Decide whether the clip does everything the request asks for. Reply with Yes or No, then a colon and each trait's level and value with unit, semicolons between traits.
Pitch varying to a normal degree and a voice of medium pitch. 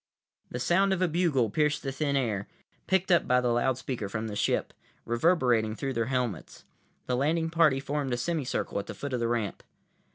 No: average, 5.0 semitones; low, 130 Hz